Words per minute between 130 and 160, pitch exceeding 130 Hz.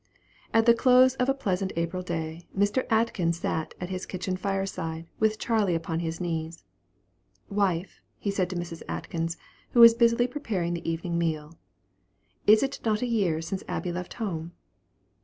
No: average, 170 wpm; medium, 185 Hz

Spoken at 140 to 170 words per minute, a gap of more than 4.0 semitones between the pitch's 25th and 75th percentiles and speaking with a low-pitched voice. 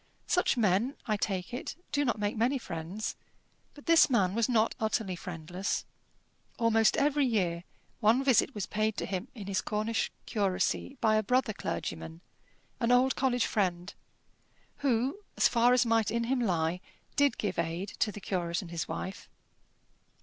No: average, 165 wpm; average, 4.8 semitones; high, 215 Hz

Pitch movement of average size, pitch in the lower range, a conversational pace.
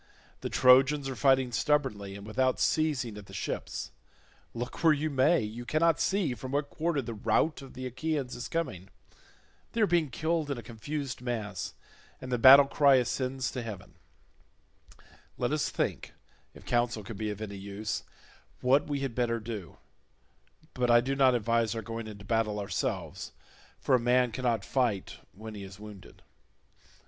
Yes: average, 4.1 semitones; low, 125 Hz; average, 170 wpm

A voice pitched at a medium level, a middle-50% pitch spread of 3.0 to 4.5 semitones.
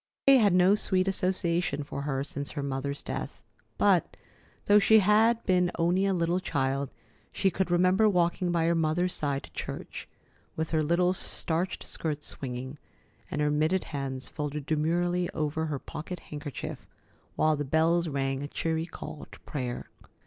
Yes: medium, 160 Hz; average, 3.9 semitones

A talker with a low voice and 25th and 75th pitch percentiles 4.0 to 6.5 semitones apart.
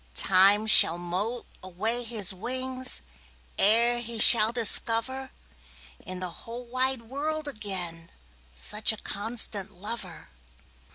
No: high, 220 Hz; average, 4.7 semitones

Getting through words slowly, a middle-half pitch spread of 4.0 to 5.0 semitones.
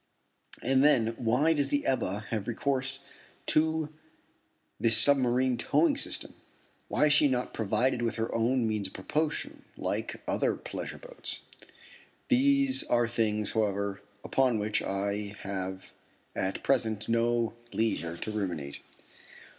Yes: slow, 130 wpm; average, 4.7 semitones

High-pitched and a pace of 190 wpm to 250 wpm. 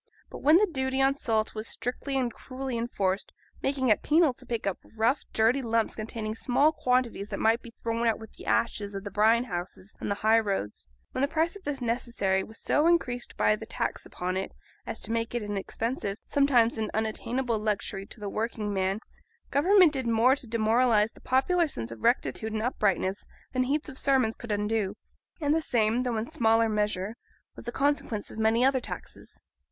Yes: high, 230 Hz; average, 200 wpm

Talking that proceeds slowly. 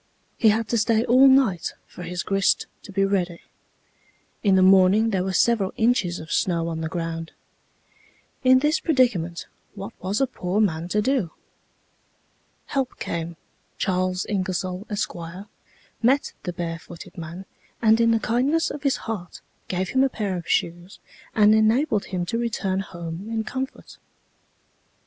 No: average, 155 wpm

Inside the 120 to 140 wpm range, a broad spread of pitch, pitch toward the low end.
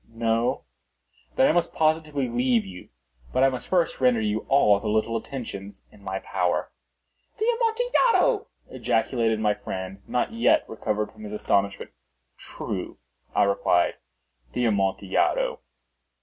Yes: slow, 135 wpm; wide, 5.9 semitones; low, 115 Hz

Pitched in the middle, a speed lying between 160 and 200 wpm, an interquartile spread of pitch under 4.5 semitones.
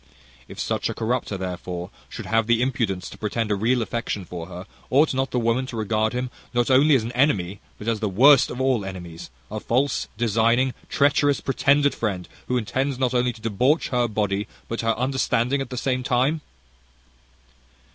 No: low, 120 Hz; average, 185 wpm; average, 3.6 semitones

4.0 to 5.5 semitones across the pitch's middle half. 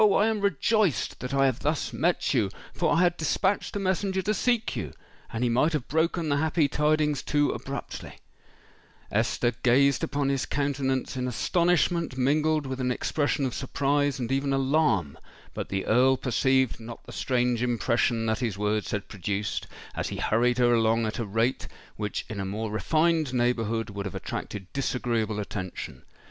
Yes: average, 4.9 semitones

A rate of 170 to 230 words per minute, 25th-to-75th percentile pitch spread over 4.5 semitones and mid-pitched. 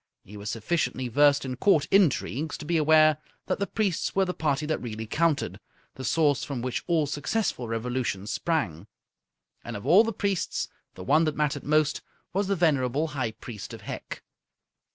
Yes: average, 175 wpm; average, 5.0 semitones; medium, 150 Hz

